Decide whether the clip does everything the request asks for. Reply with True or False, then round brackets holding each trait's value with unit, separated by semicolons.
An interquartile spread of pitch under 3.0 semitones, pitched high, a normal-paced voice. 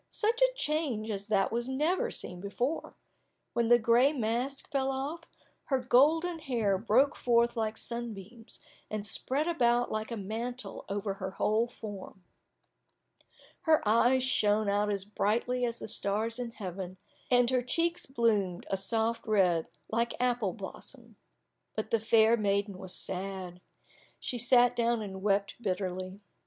False (3.7 semitones; 230 Hz; 145 wpm)